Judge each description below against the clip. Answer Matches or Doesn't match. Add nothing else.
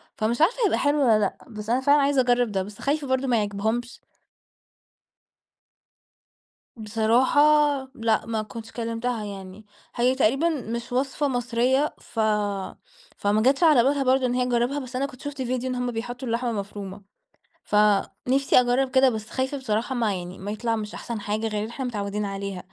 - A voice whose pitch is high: Matches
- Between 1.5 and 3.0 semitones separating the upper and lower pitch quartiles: Doesn't match